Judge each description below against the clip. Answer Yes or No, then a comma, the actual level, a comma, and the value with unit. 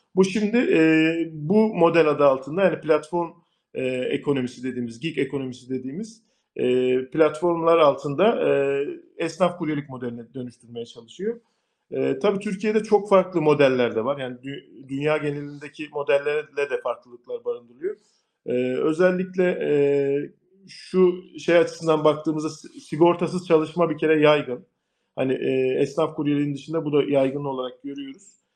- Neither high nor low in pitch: Yes, medium, 155 Hz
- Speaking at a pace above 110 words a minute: Yes, average, 130 wpm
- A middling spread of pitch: Yes, average, 4.6 semitones